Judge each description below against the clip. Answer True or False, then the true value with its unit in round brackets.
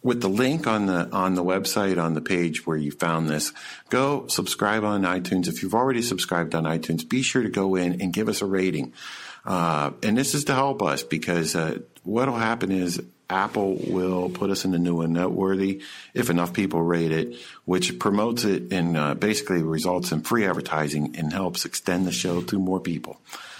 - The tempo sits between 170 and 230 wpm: True (205 wpm)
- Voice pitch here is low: True (90 Hz)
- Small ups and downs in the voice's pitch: False (3.1 semitones)